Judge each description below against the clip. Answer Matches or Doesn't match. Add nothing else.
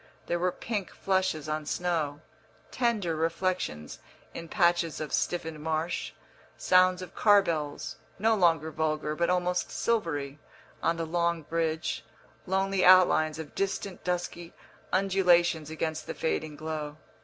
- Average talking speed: Doesn't match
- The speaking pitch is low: Doesn't match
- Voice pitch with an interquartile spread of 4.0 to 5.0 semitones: Doesn't match